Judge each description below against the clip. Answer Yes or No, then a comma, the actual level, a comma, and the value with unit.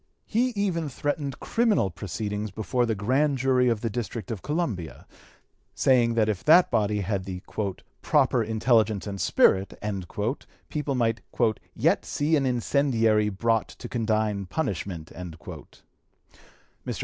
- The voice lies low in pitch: Yes, low, 115 Hz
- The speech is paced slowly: Yes, slow, 125 wpm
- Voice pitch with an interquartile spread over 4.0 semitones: Yes, average, 4.8 semitones